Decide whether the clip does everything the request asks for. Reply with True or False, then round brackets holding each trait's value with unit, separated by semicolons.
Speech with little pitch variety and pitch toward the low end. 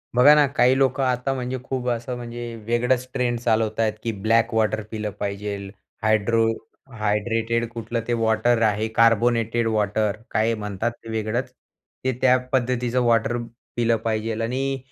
True (2.0 semitones; 115 Hz)